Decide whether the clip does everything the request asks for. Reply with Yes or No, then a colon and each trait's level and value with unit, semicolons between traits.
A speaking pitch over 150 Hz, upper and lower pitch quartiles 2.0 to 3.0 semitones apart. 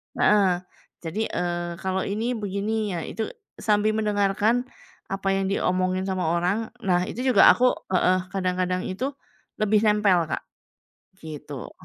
Yes: high, 190 Hz; average, 2.7 semitones